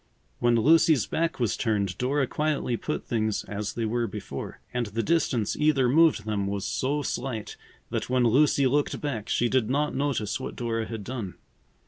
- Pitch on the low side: Yes, low, 120 Hz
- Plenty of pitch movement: No, average, 4.7 semitones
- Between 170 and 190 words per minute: Yes, average, 175 wpm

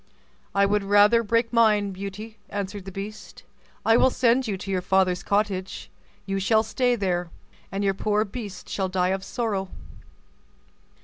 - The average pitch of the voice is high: Yes, high, 200 Hz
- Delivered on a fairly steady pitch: Yes, narrow, 2.3 semitones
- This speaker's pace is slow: No, average, 160 wpm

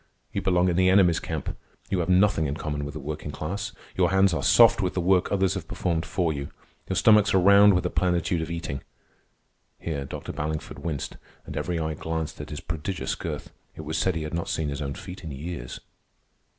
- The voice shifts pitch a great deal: No, average, 3.3 semitones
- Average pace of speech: No, fast, 215 wpm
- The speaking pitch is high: No, very low, 85 Hz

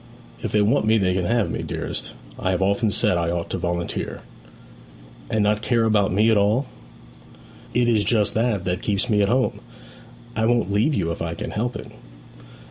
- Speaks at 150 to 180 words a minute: No, average, 200 wpm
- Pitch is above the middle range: No, low, 105 Hz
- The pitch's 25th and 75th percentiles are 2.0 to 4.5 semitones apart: Yes, average, 3.3 semitones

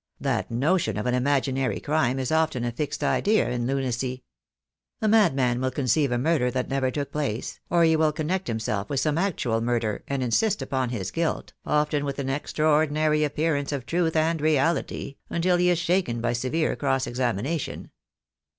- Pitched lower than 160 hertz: Yes, medium, 140 Hz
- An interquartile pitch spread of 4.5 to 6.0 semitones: No, average, 4.1 semitones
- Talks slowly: No, average, 180 wpm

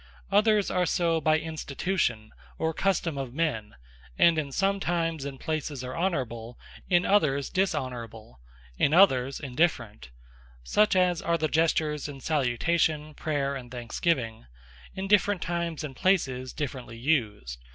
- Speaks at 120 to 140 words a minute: Yes, slow, 135 wpm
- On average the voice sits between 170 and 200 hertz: No, medium, 150 Hz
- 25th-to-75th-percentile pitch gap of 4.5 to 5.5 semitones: Yes, average, 5.1 semitones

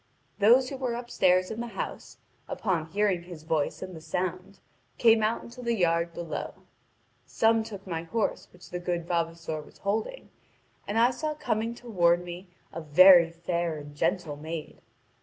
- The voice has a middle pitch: Yes, medium, 180 Hz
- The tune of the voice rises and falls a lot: No, average, 4.9 semitones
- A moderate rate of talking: Yes, average, 165 wpm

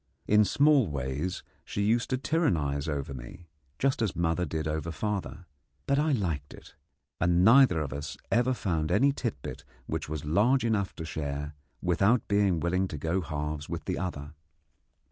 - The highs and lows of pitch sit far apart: Yes, wide, 6.3 semitones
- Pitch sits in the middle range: No, very low, 90 Hz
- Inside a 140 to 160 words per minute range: No, average, 170 wpm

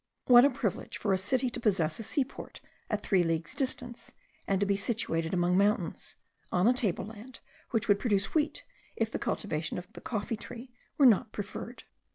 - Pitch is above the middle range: Yes, high, 210 Hz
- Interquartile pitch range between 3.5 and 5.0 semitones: Yes, average, 4.3 semitones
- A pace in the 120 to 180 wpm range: No, average, 190 wpm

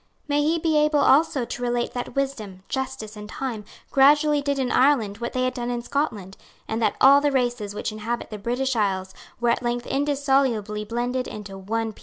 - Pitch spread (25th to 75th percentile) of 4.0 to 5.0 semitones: Yes, average, 4.3 semitones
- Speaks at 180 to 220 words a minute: Yes, average, 200 wpm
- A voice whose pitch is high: Yes, high, 245 Hz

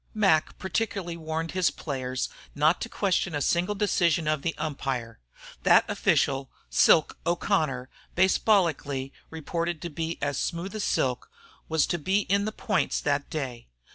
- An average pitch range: Yes, average, 4.6 semitones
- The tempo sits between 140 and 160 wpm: Yes, average, 150 wpm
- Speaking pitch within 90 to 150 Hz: No, medium, 165 Hz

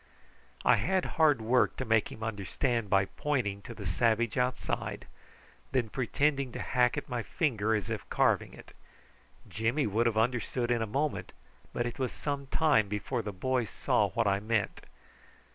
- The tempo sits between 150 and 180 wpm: Yes, average, 175 wpm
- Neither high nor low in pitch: No, low, 120 Hz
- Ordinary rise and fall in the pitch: Yes, average, 3.3 semitones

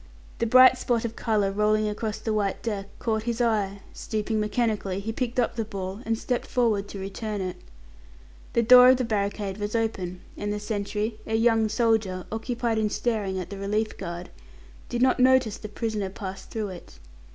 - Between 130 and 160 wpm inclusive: No, average, 185 wpm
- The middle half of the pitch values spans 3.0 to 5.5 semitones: No, narrow, 2.5 semitones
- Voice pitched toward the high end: Yes, high, 215 Hz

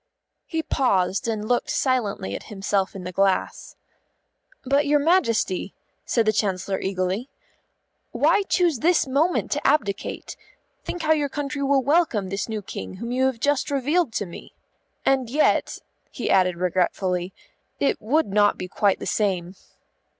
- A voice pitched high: Yes, high, 225 Hz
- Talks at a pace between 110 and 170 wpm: Yes, average, 150 wpm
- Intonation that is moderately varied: No, wide, 6.8 semitones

